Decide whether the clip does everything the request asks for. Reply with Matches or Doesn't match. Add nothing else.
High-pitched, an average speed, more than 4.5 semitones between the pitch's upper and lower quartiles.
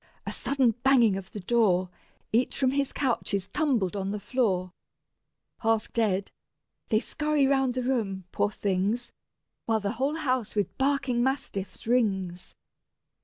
Matches